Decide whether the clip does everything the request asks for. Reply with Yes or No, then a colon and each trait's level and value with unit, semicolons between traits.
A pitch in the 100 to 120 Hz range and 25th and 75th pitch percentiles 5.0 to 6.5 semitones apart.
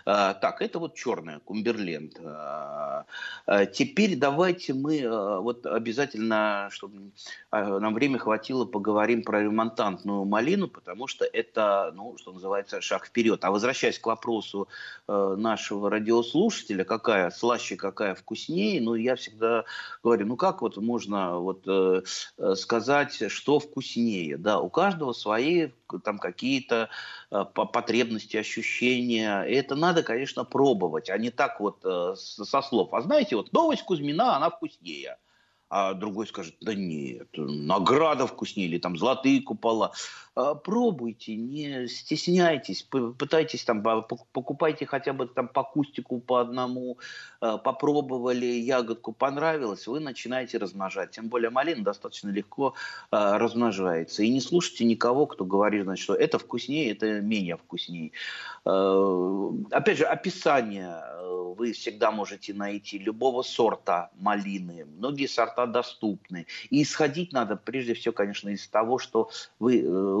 Yes: low, 115 Hz; average, 5.3 semitones